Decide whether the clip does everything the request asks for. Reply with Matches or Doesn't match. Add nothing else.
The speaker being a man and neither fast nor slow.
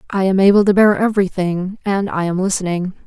Doesn't match